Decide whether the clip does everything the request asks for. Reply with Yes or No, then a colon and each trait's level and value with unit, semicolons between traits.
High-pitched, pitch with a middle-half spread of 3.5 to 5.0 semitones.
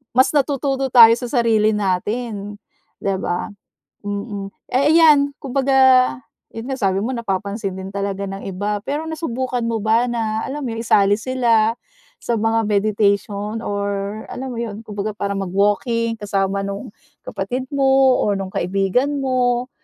Yes: high, 220 Hz; average, 4.0 semitones